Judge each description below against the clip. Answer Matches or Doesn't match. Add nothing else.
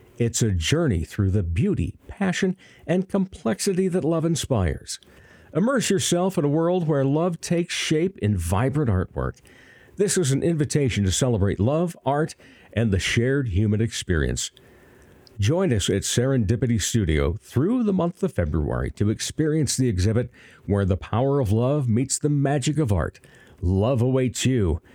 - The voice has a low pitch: Matches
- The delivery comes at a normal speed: Matches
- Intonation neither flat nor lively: Doesn't match